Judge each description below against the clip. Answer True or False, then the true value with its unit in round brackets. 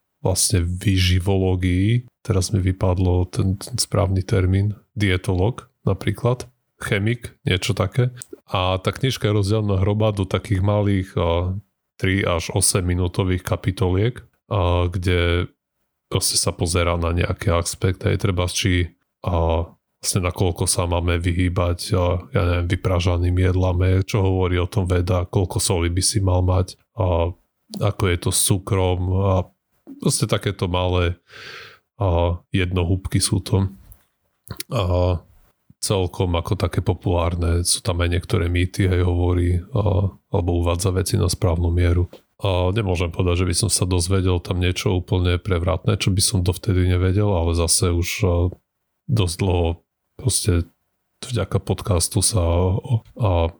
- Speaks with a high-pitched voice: False (95 Hz)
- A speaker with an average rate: True (140 wpm)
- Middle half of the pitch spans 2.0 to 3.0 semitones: True (2.5 semitones)